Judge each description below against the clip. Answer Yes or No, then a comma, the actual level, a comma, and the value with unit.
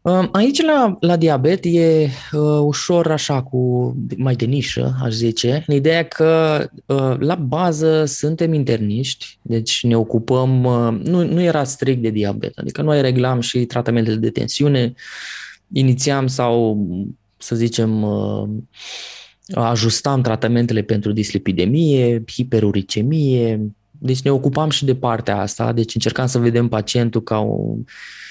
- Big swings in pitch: No, average, 4.6 semitones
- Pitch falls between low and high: No, low, 125 Hz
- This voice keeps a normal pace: Yes, average, 135 wpm